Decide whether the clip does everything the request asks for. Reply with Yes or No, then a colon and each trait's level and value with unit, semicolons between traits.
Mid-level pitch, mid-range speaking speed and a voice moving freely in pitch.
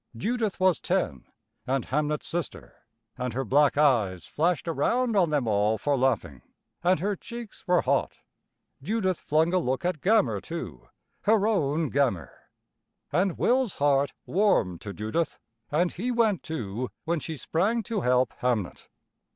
Yes: medium, 155 Hz; average, 150 wpm; wide, 7.0 semitones